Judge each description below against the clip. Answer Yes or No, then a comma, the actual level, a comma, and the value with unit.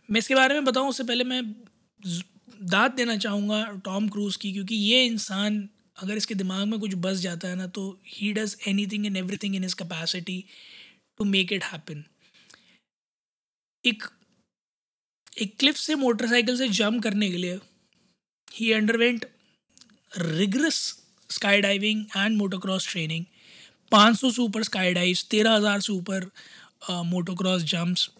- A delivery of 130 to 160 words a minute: Yes, average, 145 wpm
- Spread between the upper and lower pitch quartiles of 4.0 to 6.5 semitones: No, average, 3.1 semitones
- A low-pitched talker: No, high, 205 Hz